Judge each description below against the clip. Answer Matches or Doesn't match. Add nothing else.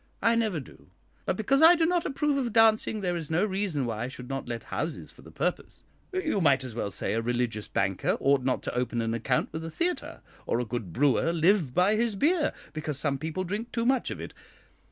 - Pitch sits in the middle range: Matches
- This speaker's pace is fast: Matches